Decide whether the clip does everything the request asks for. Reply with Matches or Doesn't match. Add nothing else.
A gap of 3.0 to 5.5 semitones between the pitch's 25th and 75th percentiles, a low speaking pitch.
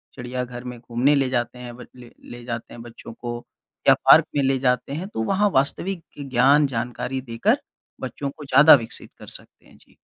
Doesn't match